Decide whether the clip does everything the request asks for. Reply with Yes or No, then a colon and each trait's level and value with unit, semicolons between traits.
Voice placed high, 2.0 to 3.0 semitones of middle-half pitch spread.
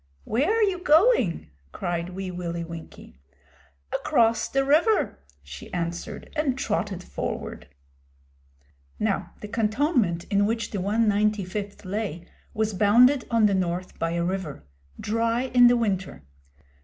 No: high, 210 Hz; average, 5.2 semitones